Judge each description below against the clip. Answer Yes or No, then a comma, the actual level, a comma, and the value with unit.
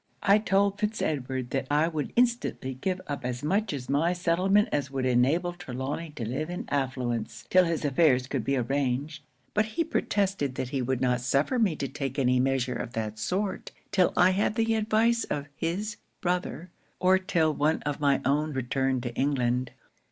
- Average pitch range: No, wide, 6.1 semitones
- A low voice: No, medium, 145 Hz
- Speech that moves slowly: No, average, 185 wpm